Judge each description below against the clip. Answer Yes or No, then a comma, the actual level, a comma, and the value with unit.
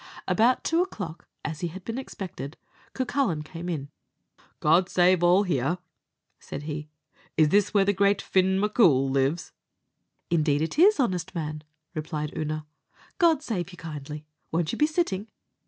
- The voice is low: No, medium, 175 Hz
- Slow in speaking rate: No, average, 155 wpm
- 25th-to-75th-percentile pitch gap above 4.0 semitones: Yes, average, 4.9 semitones